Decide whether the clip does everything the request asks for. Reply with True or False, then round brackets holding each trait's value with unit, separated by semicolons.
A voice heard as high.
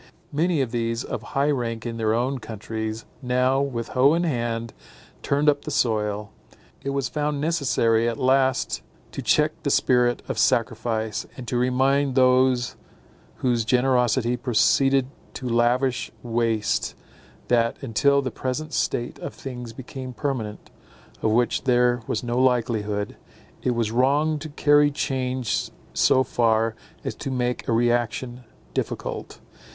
False (125 Hz)